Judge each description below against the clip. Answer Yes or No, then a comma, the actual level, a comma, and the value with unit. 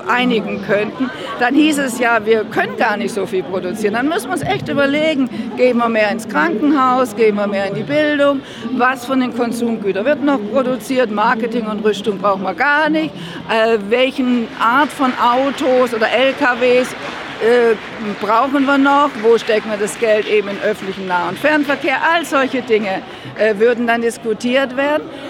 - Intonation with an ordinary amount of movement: Yes, average, 4.1 semitones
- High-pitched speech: Yes, high, 240 Hz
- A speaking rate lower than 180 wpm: Yes, average, 170 wpm